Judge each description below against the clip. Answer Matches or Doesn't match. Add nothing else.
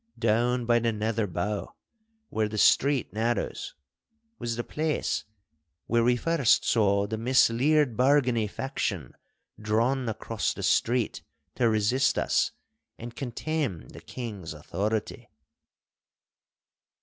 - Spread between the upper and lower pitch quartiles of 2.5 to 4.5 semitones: Matches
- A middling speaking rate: Doesn't match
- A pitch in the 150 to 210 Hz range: Doesn't match